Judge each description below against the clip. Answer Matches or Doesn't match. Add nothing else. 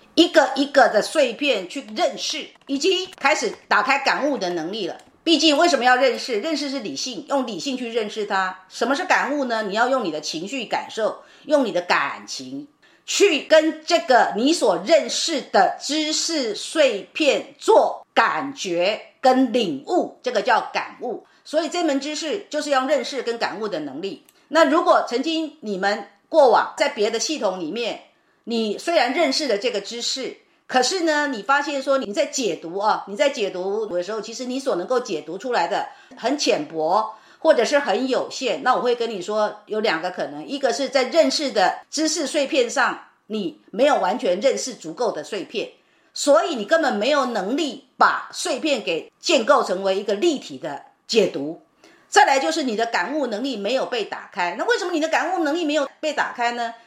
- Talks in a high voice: Matches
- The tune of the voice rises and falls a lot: Doesn't match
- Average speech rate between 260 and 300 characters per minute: Matches